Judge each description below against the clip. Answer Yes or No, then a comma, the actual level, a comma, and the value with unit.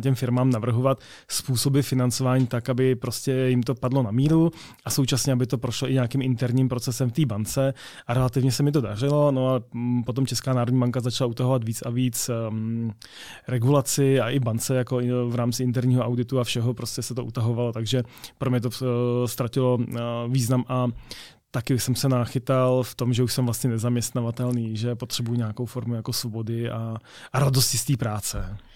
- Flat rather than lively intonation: Yes, narrow, 1.5 semitones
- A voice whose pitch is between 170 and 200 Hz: No, low, 125 Hz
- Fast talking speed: Yes, fast, 190 wpm